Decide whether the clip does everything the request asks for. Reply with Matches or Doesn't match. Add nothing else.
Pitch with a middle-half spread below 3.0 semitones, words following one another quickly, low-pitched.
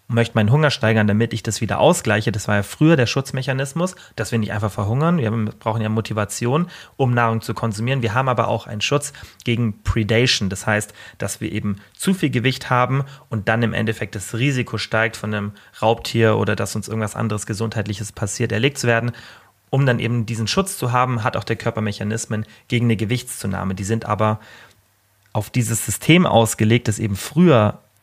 Matches